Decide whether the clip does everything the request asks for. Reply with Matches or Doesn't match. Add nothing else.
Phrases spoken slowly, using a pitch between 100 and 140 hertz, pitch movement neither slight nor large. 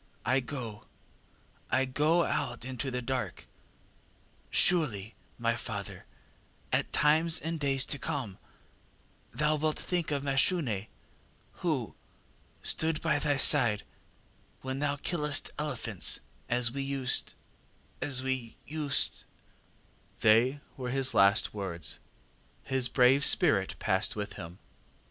Matches